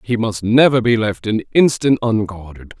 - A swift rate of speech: No, average, 170 wpm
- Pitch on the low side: Yes, low, 110 Hz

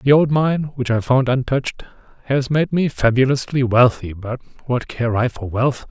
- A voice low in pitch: Yes, low, 130 Hz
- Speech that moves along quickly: No, average, 185 wpm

